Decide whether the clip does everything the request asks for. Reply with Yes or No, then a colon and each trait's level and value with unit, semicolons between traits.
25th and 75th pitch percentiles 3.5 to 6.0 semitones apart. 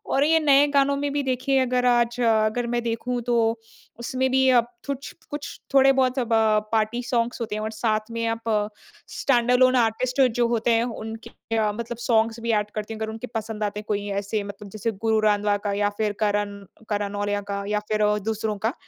No: average, 2.8 semitones